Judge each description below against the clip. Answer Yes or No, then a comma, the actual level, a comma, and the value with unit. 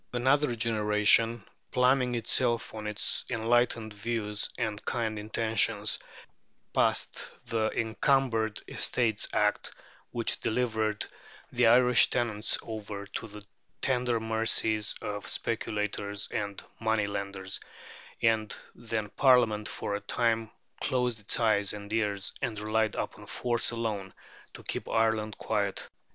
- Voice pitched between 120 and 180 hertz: No, low, 110 Hz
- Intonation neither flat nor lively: No, narrow, 1.9 semitones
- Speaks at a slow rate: Yes, slow, 115 wpm